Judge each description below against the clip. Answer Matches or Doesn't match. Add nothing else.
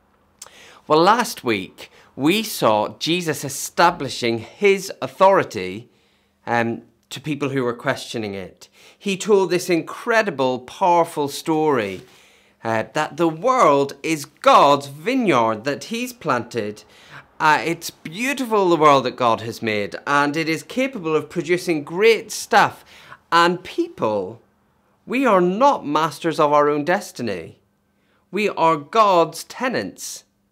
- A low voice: Doesn't match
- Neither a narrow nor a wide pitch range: Doesn't match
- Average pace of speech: Doesn't match